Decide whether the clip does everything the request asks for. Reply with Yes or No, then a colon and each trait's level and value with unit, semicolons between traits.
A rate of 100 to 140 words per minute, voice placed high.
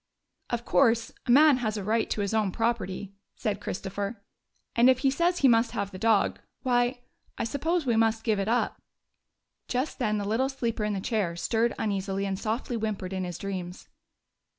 No: average, 195 wpm; high, 225 Hz